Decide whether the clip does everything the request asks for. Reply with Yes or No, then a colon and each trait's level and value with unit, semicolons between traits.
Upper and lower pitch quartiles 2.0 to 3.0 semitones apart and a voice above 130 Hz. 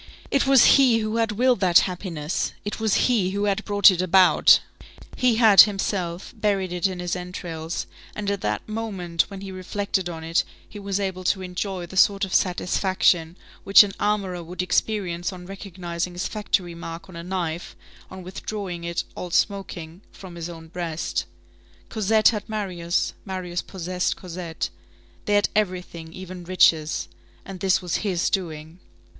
Yes: narrow, 2.6 semitones; medium, 185 Hz